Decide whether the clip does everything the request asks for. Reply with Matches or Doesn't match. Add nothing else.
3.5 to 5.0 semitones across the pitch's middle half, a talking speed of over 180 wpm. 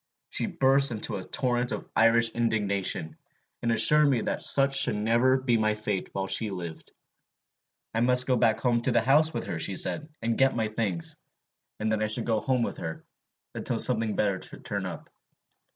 Doesn't match